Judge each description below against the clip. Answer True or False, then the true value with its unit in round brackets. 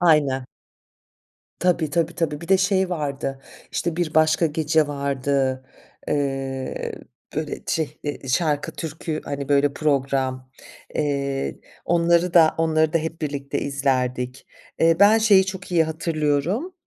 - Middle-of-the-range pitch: True (155 Hz)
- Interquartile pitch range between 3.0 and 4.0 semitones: True (3.3 semitones)